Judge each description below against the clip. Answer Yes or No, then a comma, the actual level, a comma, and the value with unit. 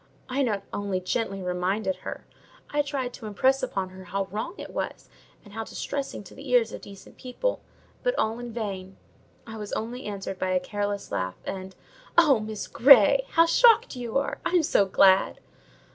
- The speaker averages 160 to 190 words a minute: Yes, average, 180 wpm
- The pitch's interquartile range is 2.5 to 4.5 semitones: No, wide, 5.5 semitones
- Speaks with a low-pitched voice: No, high, 220 Hz